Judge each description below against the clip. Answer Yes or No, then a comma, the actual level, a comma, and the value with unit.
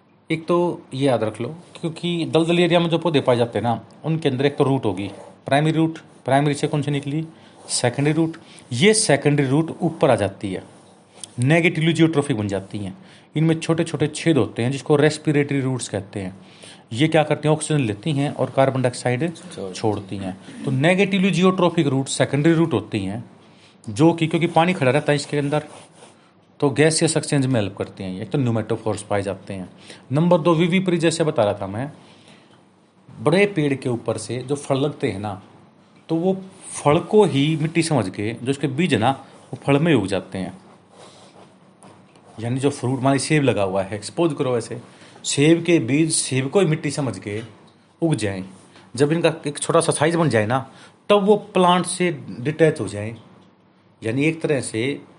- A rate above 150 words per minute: Yes, fast, 190 wpm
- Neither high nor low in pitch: Yes, medium, 145 Hz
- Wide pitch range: Yes, wide, 6.0 semitones